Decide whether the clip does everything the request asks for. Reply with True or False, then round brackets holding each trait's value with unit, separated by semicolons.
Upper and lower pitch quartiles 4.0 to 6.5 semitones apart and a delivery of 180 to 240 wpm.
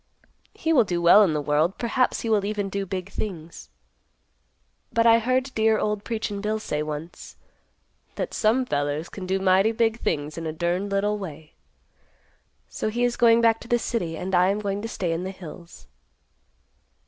True (4.6 semitones; 185 wpm)